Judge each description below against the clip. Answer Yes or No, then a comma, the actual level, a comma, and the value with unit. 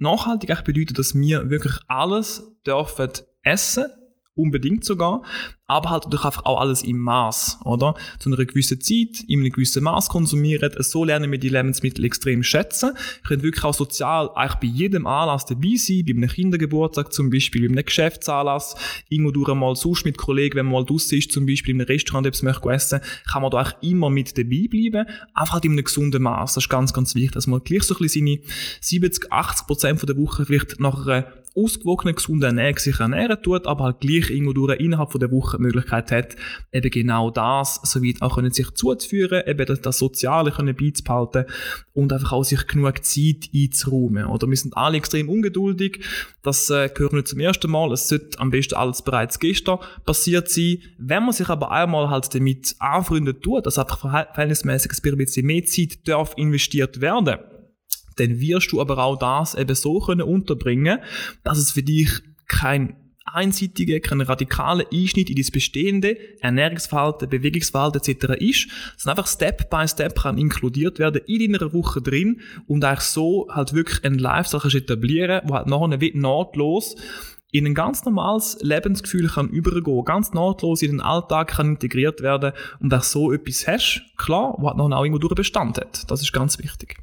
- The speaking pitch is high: No, medium, 145 Hz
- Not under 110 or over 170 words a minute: No, average, 185 wpm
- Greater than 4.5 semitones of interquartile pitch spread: No, average, 4.2 semitones